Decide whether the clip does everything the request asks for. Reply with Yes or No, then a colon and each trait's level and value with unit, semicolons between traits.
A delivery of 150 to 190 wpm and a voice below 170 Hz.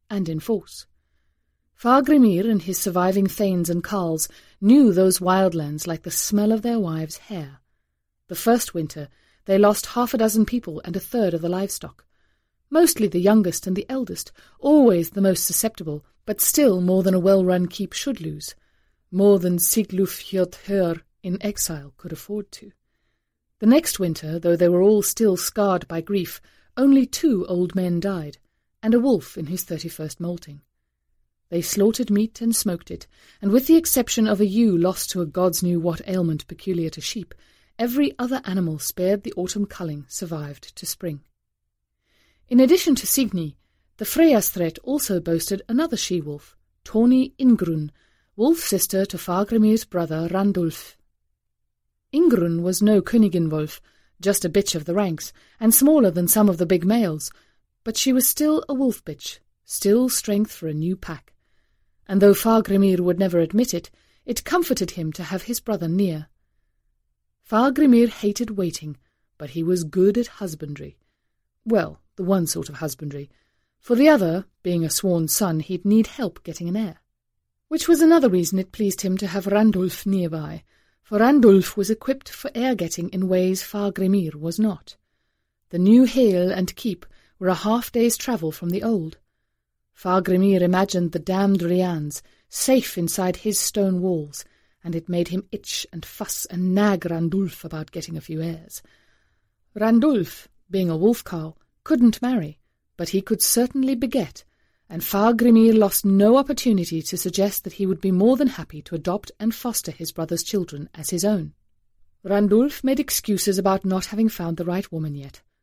No: average, 170 wpm; high, 190 Hz